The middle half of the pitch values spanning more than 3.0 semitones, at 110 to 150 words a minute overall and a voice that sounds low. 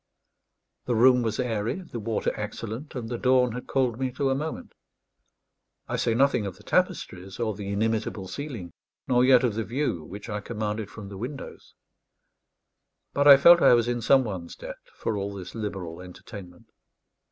No: average, 4.0 semitones; average, 175 wpm; low, 115 Hz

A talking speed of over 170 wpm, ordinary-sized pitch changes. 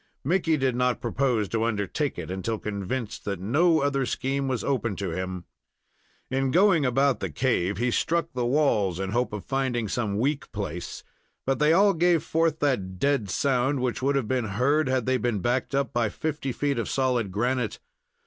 Yes: average, 190 wpm; average, 4.8 semitones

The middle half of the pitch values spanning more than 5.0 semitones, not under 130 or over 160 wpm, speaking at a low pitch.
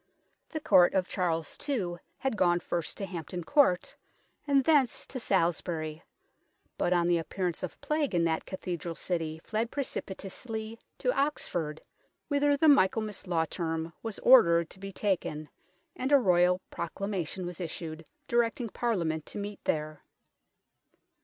No: wide, 5.4 semitones; average, 140 wpm; medium, 185 Hz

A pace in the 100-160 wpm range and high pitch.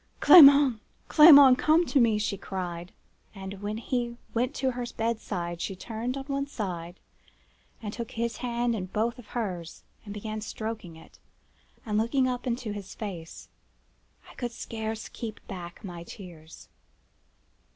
Yes: average, 150 wpm; high, 220 Hz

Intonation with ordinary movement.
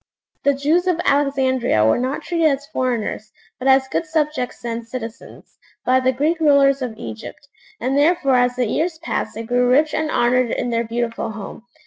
Yes: average, 3.5 semitones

